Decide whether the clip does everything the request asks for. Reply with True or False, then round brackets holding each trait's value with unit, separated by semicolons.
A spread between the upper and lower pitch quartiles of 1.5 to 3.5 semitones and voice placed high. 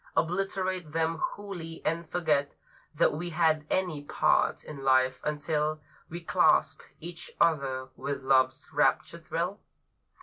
False (3.1 semitones; 160 Hz)